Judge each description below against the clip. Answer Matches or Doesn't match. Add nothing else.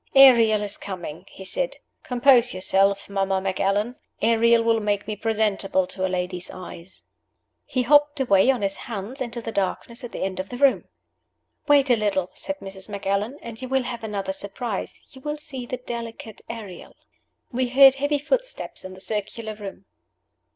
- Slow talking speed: Doesn't match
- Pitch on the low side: Doesn't match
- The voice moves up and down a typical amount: Matches